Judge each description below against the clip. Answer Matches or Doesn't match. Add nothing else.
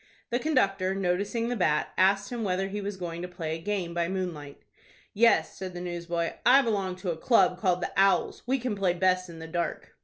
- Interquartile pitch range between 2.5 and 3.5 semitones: Matches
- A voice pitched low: Doesn't match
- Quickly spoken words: Matches